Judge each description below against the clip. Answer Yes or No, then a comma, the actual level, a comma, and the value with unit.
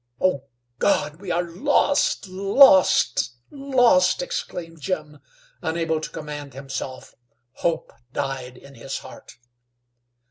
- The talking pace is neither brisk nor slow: No, slow, 105 wpm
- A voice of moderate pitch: Yes, medium, 165 Hz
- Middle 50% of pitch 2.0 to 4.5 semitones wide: No, wide, 5.6 semitones